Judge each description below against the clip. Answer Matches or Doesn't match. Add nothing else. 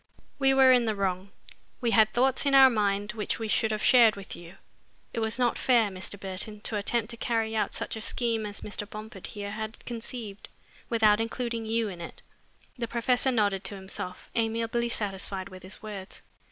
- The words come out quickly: Doesn't match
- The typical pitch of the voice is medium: Doesn't match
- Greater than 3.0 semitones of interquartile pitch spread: Doesn't match